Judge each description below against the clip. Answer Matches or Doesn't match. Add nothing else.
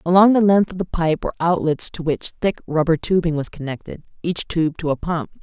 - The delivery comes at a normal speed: Doesn't match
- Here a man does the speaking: Doesn't match